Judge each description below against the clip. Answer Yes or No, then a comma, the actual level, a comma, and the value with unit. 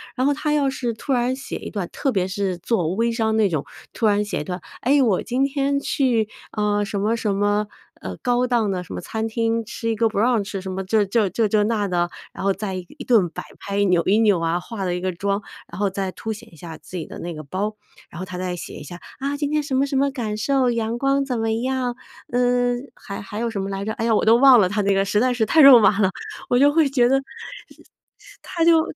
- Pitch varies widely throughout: No, average, 4.2 semitones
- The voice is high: Yes, high, 220 Hz